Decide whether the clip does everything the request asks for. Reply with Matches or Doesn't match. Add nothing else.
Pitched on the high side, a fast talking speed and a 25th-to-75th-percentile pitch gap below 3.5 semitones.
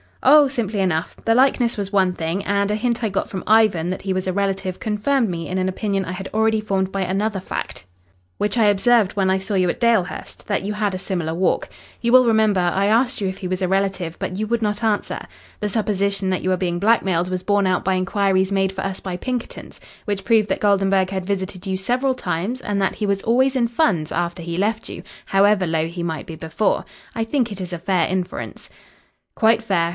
Matches